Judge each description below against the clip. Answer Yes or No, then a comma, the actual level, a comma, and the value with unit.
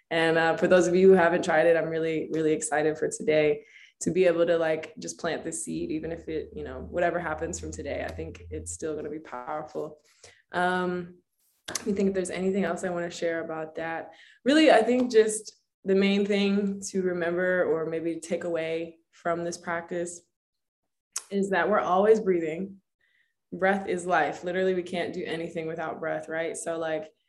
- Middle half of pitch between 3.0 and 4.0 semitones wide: No, narrow, 2.6 semitones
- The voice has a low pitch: No, medium, 170 Hz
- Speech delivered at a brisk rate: No, average, 195 wpm